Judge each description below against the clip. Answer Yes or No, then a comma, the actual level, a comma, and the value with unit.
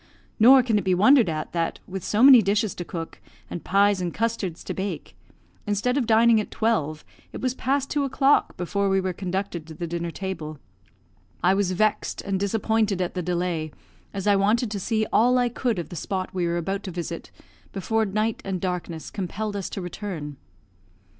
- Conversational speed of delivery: Yes, average, 195 wpm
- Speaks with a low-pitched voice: No, high, 195 Hz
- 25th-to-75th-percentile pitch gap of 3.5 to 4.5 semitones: Yes, average, 3.8 semitones